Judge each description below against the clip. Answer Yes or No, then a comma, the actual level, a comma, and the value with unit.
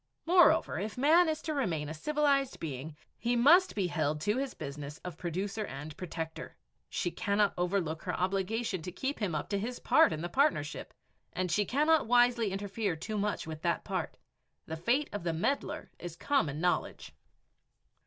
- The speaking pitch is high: Yes, high, 195 Hz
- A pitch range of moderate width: No, wide, 7.4 semitones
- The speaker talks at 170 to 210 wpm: Yes, average, 175 wpm